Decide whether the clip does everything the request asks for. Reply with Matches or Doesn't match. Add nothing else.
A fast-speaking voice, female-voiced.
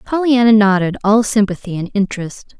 Doesn't match